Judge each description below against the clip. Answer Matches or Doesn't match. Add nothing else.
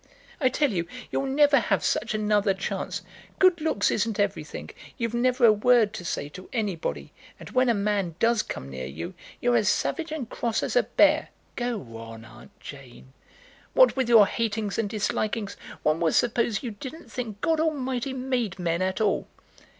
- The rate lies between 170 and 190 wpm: Matches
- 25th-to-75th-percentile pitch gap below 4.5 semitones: Doesn't match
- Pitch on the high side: Matches